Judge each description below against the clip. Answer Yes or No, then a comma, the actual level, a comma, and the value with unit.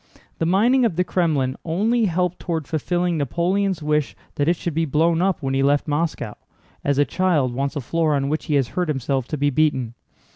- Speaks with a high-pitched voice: No, medium, 155 Hz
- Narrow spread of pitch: No, average, 3.9 semitones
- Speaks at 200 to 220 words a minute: Yes, fast, 205 wpm